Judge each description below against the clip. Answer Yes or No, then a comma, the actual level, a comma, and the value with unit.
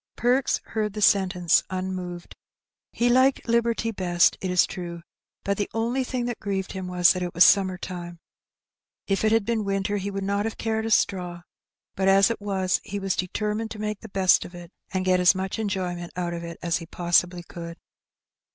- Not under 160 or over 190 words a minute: No, fast, 205 wpm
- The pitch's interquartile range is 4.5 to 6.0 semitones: No, average, 3.2 semitones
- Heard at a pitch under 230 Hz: Yes, high, 190 Hz